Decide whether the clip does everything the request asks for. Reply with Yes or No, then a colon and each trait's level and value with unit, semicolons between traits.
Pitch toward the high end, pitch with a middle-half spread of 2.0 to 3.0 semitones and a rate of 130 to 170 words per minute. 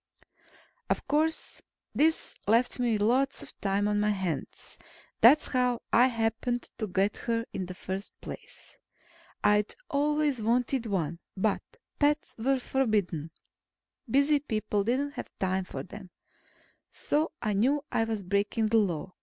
No: high, 225 Hz; average, 4.8 semitones; average, 145 wpm